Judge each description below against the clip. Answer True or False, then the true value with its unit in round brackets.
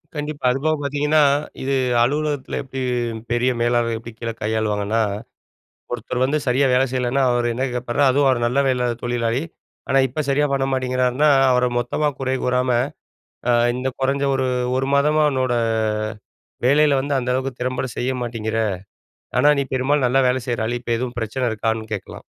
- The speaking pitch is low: True (130 Hz)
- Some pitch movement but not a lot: False (2.2 semitones)